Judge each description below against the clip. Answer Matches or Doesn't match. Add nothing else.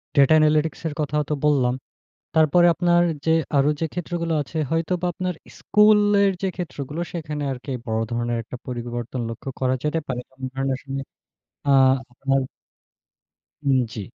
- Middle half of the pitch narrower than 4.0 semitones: Doesn't match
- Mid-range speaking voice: Matches